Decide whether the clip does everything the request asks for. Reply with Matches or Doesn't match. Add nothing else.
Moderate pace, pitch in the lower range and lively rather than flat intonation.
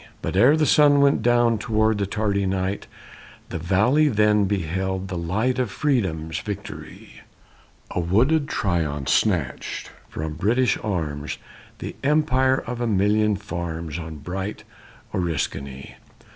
Doesn't match